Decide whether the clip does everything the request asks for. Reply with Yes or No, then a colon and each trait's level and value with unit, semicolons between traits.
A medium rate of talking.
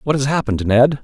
No: fast, 230 wpm